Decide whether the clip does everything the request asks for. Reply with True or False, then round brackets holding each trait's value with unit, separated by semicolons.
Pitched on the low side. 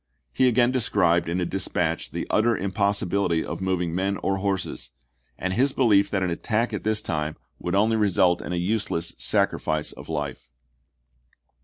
True (95 Hz)